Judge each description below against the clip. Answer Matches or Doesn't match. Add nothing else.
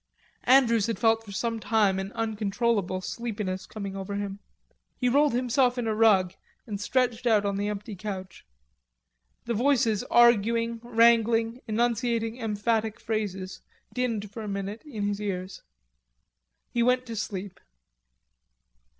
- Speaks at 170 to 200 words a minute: Doesn't match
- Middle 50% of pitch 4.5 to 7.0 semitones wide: Doesn't match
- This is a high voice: Matches